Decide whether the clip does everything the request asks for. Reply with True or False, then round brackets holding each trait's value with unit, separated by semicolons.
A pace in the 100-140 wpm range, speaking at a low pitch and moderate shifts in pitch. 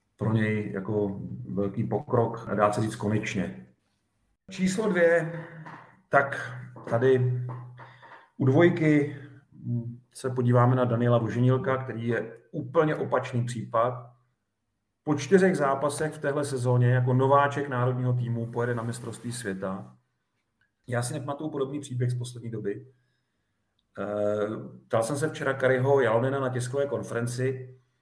True (120 wpm; 125 Hz; 4.0 semitones)